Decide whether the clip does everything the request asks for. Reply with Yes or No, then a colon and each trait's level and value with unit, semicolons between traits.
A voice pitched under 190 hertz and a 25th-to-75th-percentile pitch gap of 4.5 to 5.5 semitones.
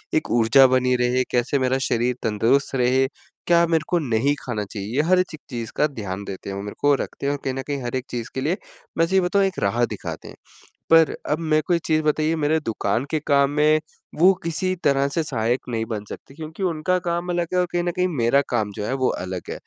Yes: medium, 140 Hz; average, 5.1 semitones